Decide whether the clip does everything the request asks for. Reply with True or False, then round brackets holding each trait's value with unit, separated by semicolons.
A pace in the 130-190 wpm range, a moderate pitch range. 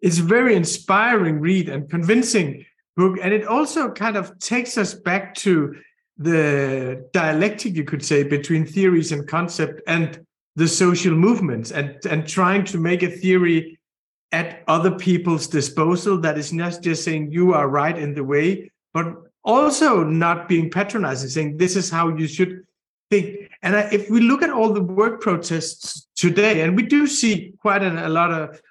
True (175 wpm; 4.0 semitones)